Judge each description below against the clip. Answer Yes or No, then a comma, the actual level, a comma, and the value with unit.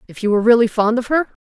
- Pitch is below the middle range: No, high, 230 Hz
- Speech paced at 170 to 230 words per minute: No, fast, 295 wpm